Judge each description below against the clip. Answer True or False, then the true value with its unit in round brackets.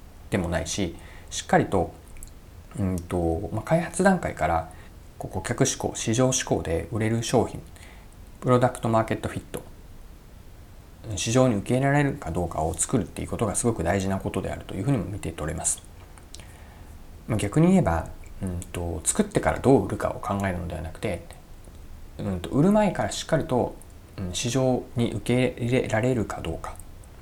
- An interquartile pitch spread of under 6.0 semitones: True (5.5 semitones)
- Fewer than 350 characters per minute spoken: True (330 characters per minute)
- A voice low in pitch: True (95 Hz)